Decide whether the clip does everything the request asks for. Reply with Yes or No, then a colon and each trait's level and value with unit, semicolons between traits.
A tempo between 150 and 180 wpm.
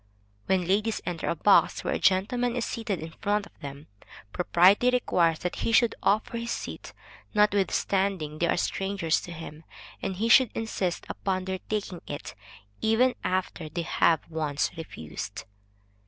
Yes: average, 155 wpm